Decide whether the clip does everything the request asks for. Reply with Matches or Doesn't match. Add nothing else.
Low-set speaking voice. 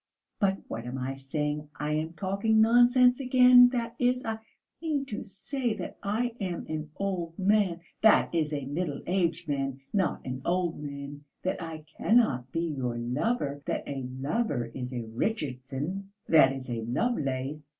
Doesn't match